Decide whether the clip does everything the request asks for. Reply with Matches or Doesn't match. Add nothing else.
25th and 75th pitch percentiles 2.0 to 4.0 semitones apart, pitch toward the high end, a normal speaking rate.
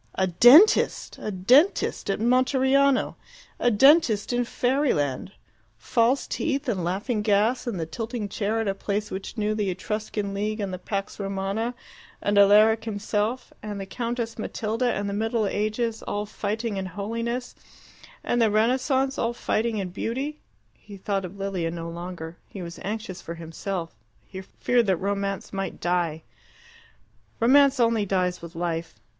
Matches